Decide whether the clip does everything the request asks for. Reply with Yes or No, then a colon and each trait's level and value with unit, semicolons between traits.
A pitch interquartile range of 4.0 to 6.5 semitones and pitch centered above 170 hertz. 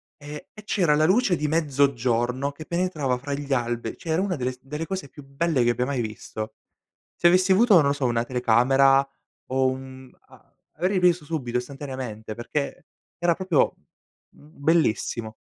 No: average, 4.8 semitones; medium, 140 Hz